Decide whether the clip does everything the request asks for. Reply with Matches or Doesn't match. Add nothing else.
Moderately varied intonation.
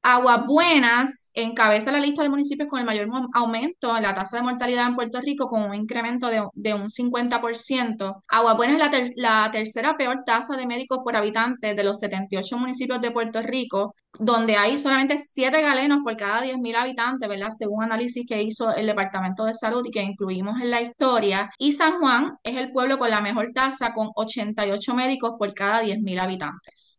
Matches